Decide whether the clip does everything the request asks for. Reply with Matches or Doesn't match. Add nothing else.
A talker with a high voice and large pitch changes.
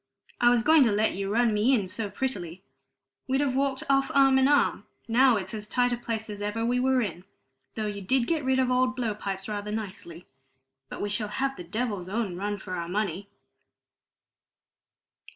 Doesn't match